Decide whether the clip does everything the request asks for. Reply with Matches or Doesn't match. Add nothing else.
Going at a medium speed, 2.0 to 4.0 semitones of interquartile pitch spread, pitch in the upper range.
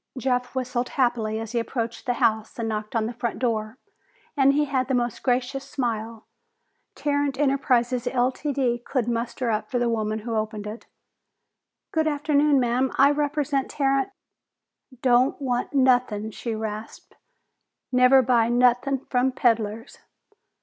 Matches